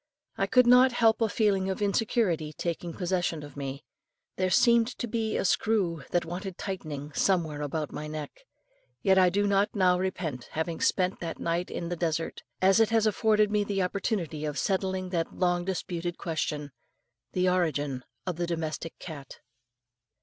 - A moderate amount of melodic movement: Yes, average, 3.8 semitones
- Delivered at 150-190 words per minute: Yes, average, 170 wpm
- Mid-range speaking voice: Yes, medium, 180 Hz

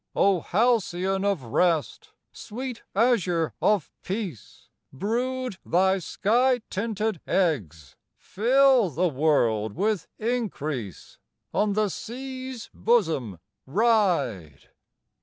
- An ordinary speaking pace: No, slow, 90 wpm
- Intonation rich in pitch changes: Yes, wide, 6.8 semitones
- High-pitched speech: Yes, high, 195 Hz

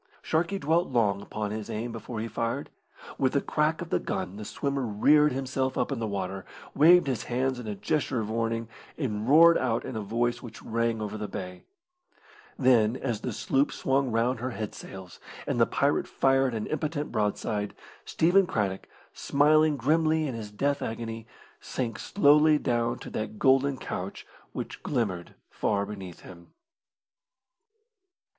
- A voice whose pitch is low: Yes, low, 120 Hz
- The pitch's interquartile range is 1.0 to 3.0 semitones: No, average, 4.7 semitones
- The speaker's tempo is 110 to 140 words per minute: No, average, 165 wpm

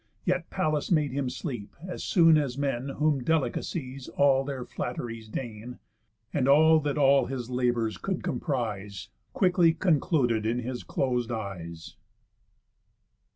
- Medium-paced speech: No, slow, 130 wpm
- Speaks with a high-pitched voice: No, low, 135 Hz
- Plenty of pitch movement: No, average, 4.2 semitones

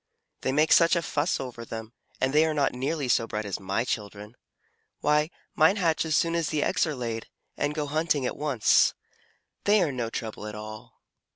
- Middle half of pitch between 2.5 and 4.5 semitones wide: No, wide, 5.5 semitones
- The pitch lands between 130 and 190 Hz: Yes, medium, 140 Hz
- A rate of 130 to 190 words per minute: No, average, 200 wpm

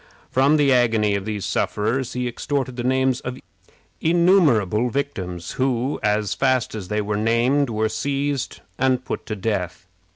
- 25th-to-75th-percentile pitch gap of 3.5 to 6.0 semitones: Yes, average, 4.1 semitones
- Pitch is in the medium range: No, low, 120 Hz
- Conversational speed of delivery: Yes, average, 155 wpm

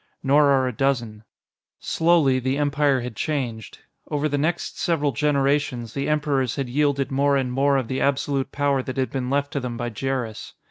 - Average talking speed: Yes, average, 185 wpm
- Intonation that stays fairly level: Yes, narrow, 2.0 semitones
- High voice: No, low, 135 Hz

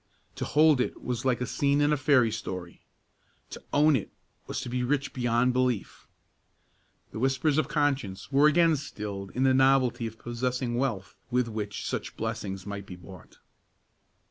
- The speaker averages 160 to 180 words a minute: Yes, average, 170 wpm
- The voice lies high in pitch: No, low, 125 Hz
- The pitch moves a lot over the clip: No, average, 3.9 semitones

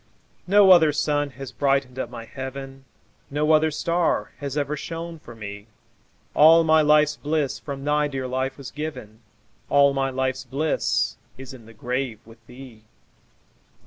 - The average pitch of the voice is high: No, medium, 140 Hz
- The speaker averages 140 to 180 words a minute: Yes, average, 155 wpm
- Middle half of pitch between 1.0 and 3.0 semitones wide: Yes, narrow, 2.6 semitones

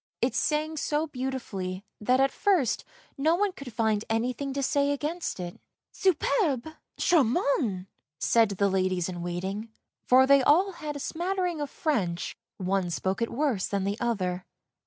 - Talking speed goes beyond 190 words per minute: No, average, 160 wpm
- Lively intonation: Yes, wide, 7.6 semitones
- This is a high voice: Yes, very high, 250 Hz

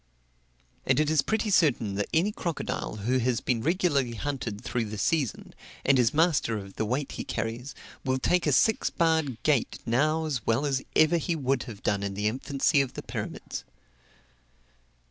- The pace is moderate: Yes, average, 180 wpm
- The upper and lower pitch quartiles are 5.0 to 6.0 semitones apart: Yes, wide, 5.6 semitones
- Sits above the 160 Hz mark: No, low, 135 Hz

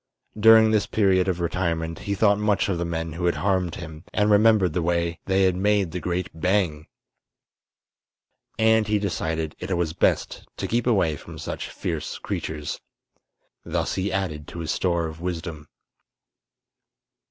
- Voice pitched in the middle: No, very low, 90 Hz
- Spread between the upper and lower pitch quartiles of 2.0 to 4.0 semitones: Yes, average, 3.7 semitones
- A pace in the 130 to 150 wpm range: No, average, 160 wpm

